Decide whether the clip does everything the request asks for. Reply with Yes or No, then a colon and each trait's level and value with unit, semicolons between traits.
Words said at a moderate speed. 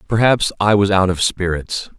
Yes: average, 180 wpm